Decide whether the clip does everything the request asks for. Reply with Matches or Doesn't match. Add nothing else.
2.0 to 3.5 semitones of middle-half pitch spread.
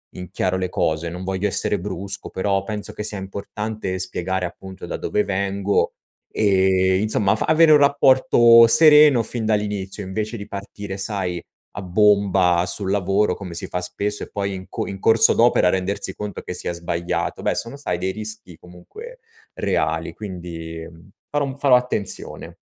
Matches